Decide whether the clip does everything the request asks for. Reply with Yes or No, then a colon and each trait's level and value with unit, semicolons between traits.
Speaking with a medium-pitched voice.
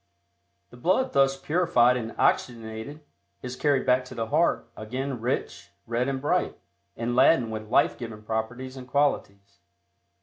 No: low, 125 Hz